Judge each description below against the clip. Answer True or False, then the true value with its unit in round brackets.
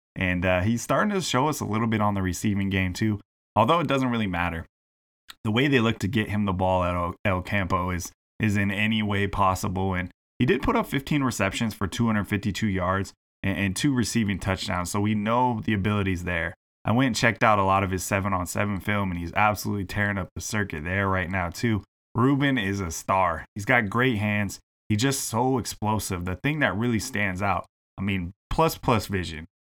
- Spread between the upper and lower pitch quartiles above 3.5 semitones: False (3.2 semitones)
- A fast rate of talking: True (215 wpm)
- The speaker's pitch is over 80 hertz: True (100 Hz)